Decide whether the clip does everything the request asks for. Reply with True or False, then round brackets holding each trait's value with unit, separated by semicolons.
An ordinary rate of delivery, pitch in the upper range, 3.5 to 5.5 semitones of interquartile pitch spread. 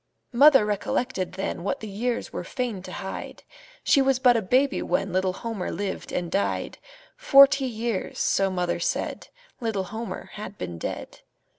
True (160 wpm; 210 Hz; 4.7 semitones)